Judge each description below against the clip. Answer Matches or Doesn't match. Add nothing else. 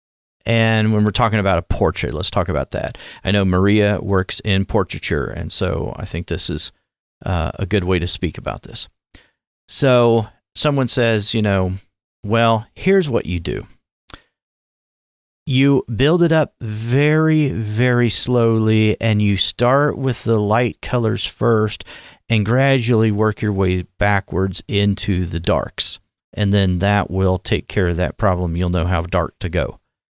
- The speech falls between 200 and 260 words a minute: Doesn't match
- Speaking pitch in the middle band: Doesn't match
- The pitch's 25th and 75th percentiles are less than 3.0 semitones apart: Doesn't match